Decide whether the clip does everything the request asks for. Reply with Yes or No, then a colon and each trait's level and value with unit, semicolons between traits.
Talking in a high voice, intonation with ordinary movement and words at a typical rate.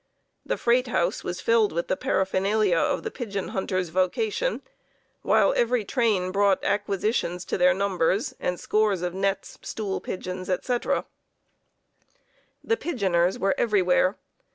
No: high, 195 Hz; average, 3.1 semitones; slow, 130 wpm